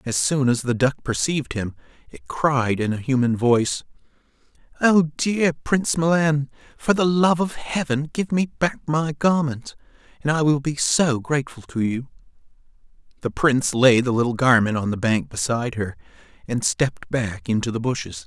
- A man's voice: Yes, male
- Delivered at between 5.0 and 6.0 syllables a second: No, 4.8 syllables/s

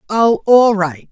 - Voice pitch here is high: Yes, high, 200 Hz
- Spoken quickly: No, average, 160 wpm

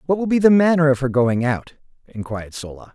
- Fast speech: Yes, fast, 225 wpm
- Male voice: Yes, male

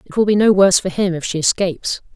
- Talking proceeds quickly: Yes, fast, 280 wpm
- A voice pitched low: No, medium, 185 Hz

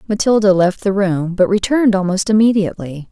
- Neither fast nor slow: Yes, average, 155 wpm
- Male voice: No, female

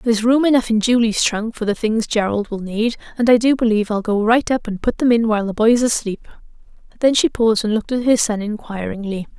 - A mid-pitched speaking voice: No, high, 225 Hz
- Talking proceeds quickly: Yes, fast, 235 wpm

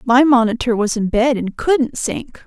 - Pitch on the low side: No, high, 245 Hz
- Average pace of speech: Yes, average, 195 wpm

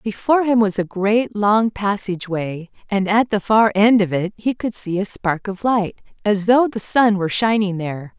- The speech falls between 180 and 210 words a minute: Yes, fast, 205 wpm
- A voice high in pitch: Yes, high, 205 Hz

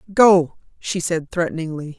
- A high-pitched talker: No, medium, 170 Hz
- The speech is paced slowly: Yes, slow, 120 wpm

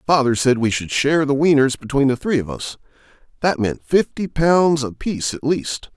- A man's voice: Yes, male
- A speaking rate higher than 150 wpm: Yes, average, 200 wpm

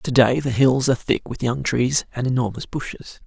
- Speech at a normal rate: No, fast, 220 wpm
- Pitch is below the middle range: Yes, low, 130 Hz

